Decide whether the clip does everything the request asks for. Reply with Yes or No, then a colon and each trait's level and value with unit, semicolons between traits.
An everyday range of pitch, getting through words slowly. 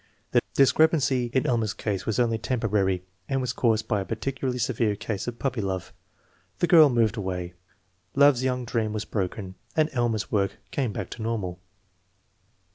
No: average, 3.7 semitones; average, 165 wpm